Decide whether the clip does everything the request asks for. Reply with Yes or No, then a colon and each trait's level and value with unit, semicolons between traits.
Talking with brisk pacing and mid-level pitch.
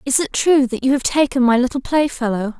No: fast, 230 wpm; very high, 260 Hz